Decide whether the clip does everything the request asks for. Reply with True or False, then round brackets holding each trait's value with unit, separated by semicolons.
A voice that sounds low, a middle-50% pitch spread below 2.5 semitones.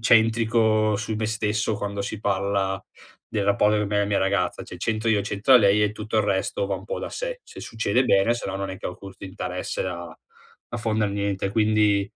True (105 Hz; 1.8 semitones)